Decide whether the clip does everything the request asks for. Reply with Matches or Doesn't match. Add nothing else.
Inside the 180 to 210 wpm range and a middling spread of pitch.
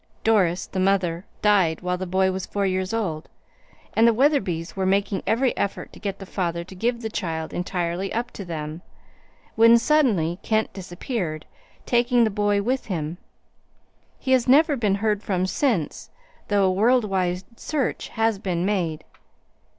Doesn't match